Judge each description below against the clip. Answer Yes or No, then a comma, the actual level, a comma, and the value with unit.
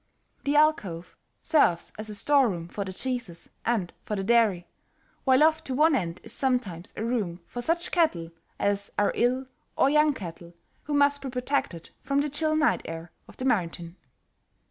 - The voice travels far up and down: Yes, wide, 8.1 semitones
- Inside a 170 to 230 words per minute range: Yes, average, 180 wpm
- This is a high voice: Yes, high, 235 Hz